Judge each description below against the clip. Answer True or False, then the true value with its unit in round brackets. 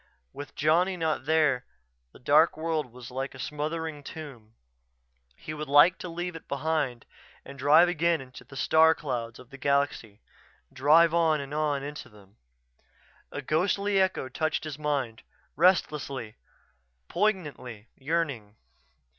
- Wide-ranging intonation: False (3.5 semitones)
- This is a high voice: False (150 Hz)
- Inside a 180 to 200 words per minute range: False (140 wpm)